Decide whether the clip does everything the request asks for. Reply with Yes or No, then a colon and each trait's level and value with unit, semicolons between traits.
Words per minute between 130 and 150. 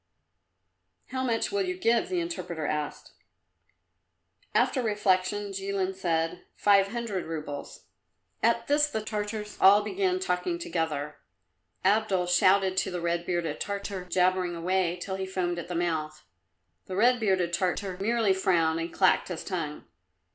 Yes: average, 140 wpm